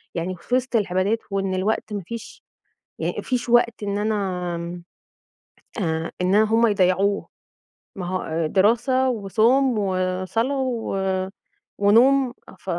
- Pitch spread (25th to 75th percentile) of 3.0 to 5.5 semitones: Yes, average, 4.0 semitones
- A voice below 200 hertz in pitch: No, high, 205 Hz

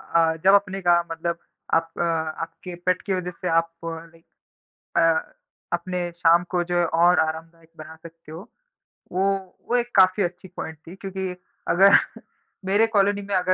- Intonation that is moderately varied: No, narrow, 2.3 semitones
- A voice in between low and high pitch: Yes, medium, 175 Hz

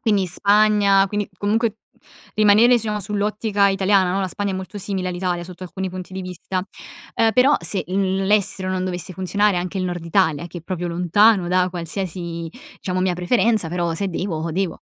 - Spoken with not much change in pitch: Yes, narrow, 2.3 semitones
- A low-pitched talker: No, high, 190 Hz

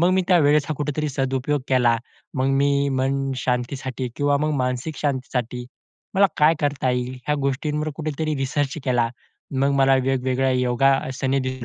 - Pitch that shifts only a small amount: Yes, narrow, 2.3 semitones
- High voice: No, low, 135 Hz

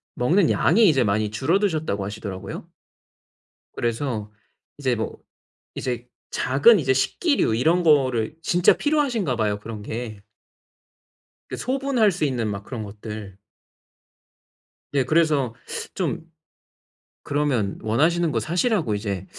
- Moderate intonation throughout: No, wide, 7.7 semitones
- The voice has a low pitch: Yes, low, 130 Hz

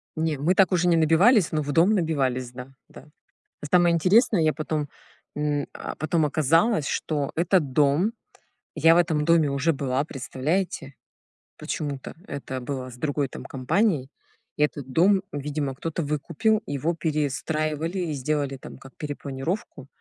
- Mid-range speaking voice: Yes, medium, 150 Hz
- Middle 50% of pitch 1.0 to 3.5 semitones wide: Yes, average, 3.2 semitones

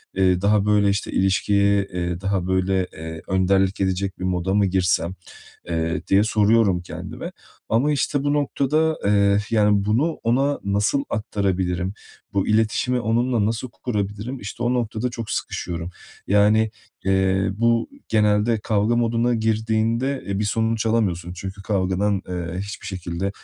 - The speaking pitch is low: Yes, low, 100 Hz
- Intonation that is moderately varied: Yes, average, 3.1 semitones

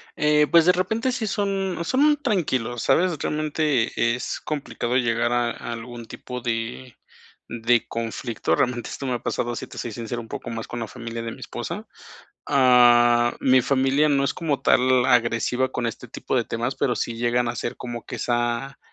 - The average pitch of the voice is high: No, low, 125 Hz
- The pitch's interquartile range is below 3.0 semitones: No, average, 3.5 semitones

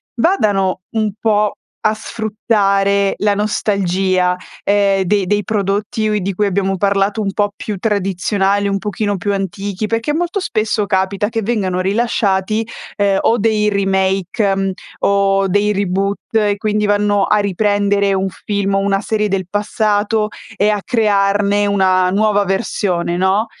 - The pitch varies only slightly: Yes, narrow, 1.5 semitones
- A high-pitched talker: Yes, high, 200 Hz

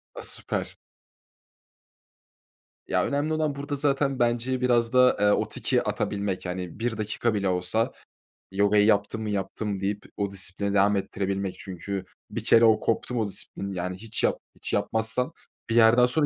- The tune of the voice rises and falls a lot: No, average, 3.6 semitones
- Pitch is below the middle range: Yes, low, 105 Hz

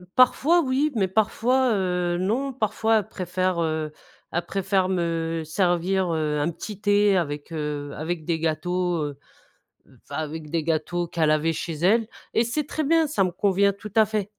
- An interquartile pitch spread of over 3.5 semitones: Yes, average, 4.7 semitones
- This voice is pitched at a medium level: Yes, medium, 180 Hz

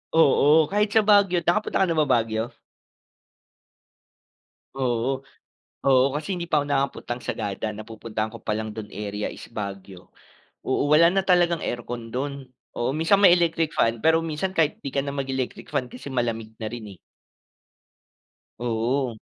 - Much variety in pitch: Yes, wide, 6.2 semitones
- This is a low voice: Yes, low, 130 Hz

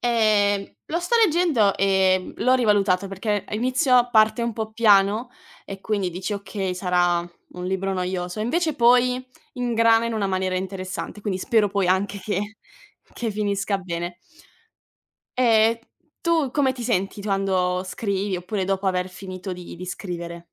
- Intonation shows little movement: No, average, 3.6 semitones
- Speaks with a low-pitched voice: No, high, 200 Hz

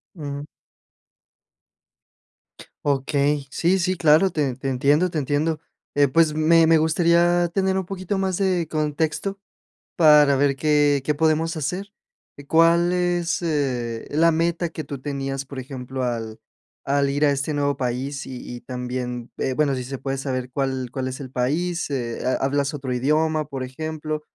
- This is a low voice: No, medium, 145 Hz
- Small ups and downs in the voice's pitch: No, average, 3.5 semitones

